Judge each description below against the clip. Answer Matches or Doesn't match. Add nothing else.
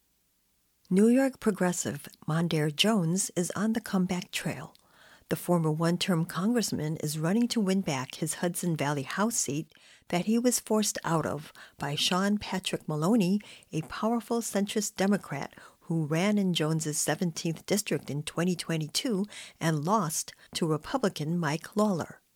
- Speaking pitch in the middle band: Matches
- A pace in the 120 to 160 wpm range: Matches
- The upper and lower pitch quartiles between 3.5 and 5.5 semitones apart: Matches